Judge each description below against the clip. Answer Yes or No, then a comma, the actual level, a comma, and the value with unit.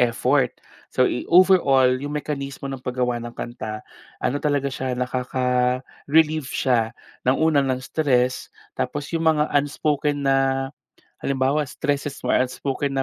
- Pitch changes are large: No, narrow, 2.4 semitones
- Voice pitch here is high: No, low, 135 Hz